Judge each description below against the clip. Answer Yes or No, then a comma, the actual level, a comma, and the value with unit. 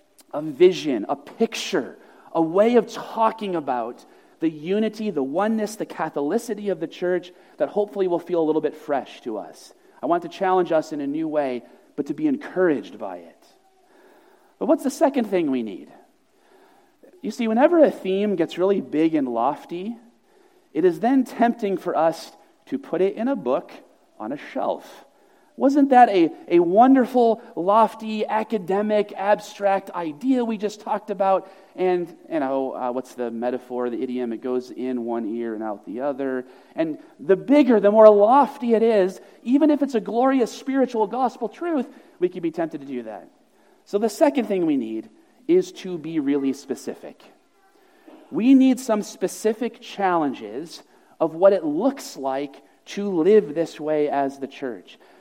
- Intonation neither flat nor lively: No, wide, 8.8 semitones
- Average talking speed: Yes, average, 170 wpm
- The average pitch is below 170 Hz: No, high, 215 Hz